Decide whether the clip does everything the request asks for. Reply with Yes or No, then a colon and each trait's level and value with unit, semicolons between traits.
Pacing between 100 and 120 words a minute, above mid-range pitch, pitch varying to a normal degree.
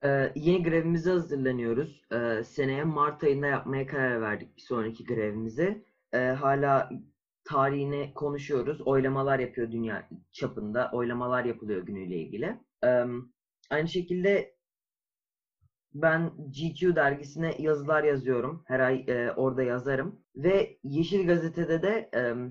No: average, 115 wpm; medium, 140 Hz; average, 4.5 semitones